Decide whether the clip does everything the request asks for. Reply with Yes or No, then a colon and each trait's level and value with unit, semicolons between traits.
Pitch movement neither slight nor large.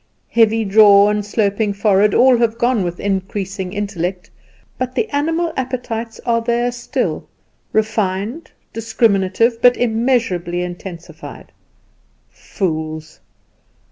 Yes: average, 3.7 semitones